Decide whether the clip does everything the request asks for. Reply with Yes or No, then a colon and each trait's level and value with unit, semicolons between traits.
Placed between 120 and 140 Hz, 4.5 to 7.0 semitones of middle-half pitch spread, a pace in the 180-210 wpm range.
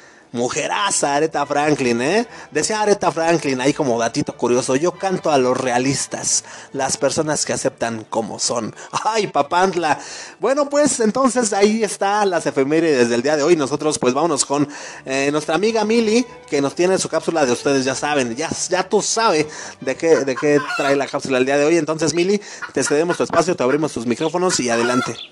No: medium, 150 Hz; wide, 5.4 semitones; fast, 190 wpm